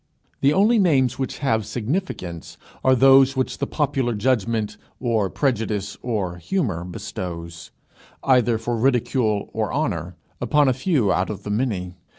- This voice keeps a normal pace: Yes, average, 145 wpm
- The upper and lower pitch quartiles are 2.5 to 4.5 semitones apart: No, average, 4.9 semitones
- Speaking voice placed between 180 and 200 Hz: No, low, 115 Hz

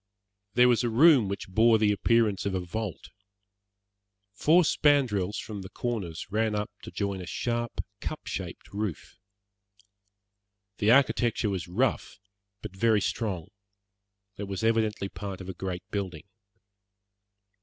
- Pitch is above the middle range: No, low, 105 Hz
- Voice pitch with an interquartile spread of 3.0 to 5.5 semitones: Yes, average, 3.3 semitones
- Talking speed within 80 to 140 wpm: Yes, slow, 135 wpm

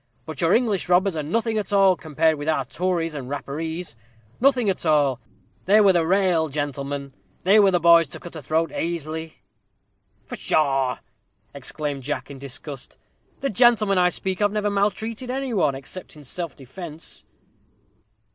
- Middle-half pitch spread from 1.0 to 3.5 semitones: No, average, 5.3 semitones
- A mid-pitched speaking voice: Yes, medium, 165 Hz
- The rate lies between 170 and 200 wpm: No, average, 160 wpm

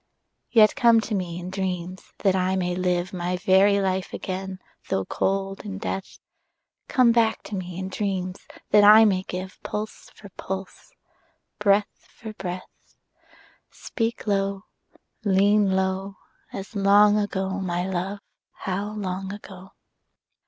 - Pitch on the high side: Yes, high, 195 Hz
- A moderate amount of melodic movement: No, narrow, 1.8 semitones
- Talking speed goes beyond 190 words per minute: No, slow, 135 wpm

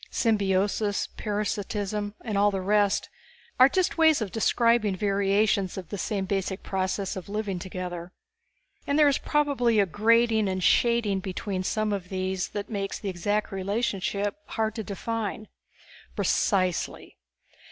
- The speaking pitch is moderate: No, high, 205 Hz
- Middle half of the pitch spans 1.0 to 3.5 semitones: Yes, narrow, 2.4 semitones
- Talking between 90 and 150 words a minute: Yes, average, 140 wpm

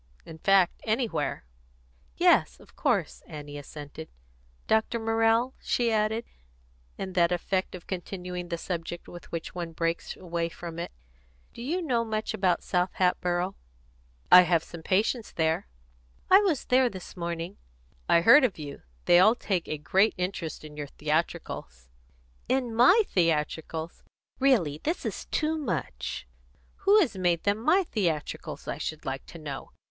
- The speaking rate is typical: Yes, average, 150 wpm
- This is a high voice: No, medium, 180 Hz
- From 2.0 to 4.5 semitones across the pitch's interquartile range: No, wide, 5.5 semitones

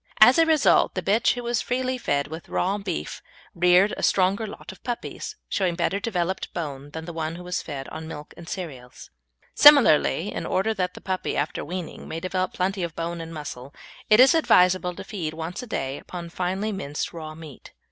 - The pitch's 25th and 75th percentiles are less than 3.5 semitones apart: No, average, 3.8 semitones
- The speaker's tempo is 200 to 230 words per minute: Yes, fast, 205 wpm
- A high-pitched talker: No, medium, 180 Hz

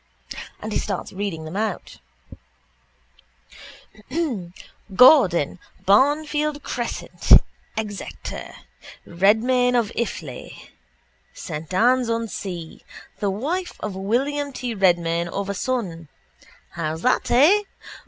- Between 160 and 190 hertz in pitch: No, high, 210 Hz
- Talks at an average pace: No, slow, 95 wpm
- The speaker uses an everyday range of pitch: No, wide, 5.9 semitones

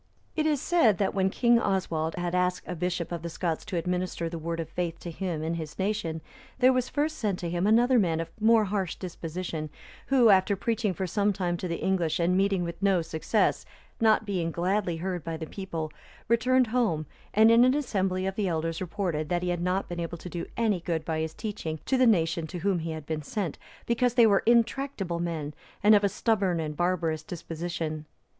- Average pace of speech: No, fast, 215 wpm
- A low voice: No, medium, 180 Hz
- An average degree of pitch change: Yes, average, 4.1 semitones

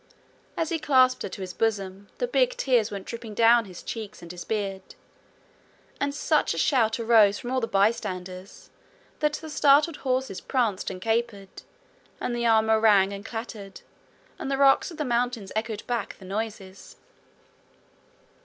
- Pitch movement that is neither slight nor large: Yes, average, 4.4 semitones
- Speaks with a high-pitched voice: Yes, high, 225 Hz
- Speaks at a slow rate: No, average, 165 wpm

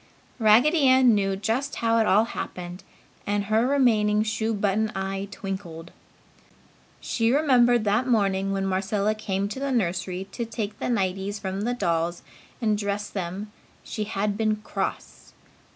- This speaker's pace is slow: No, average, 150 wpm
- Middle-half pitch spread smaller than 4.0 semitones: Yes, average, 2.8 semitones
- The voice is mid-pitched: No, high, 210 Hz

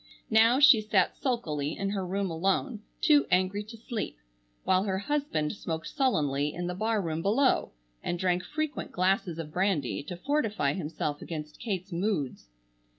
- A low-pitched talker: No, high, 190 Hz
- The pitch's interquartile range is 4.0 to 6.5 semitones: Yes, average, 5.1 semitones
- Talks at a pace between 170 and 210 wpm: No, average, 150 wpm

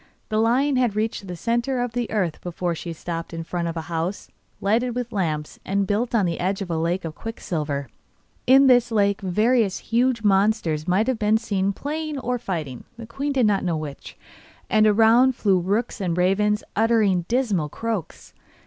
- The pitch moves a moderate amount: Yes, average, 4.9 semitones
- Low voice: No, high, 210 Hz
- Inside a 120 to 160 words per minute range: No, average, 185 wpm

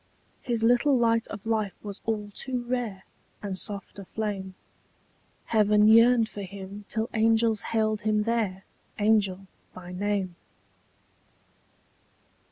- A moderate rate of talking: No, slow, 120 wpm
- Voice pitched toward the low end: No, high, 215 Hz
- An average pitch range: No, narrow, 2.3 semitones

